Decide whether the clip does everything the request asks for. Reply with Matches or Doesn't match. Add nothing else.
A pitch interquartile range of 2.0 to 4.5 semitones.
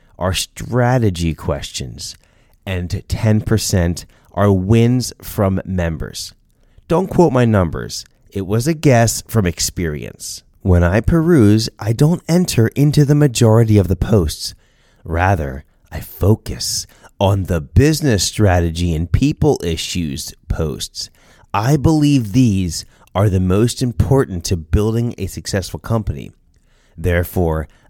Doesn't match